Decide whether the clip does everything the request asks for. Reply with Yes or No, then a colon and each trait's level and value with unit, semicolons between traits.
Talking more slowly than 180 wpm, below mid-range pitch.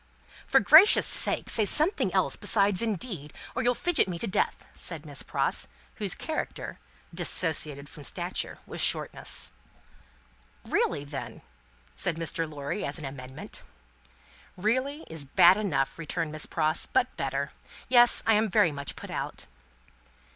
No: average, 140 wpm; medium, 170 Hz